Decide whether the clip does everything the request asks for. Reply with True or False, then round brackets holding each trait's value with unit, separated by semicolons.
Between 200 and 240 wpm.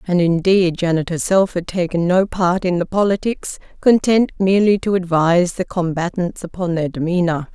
False (160 wpm)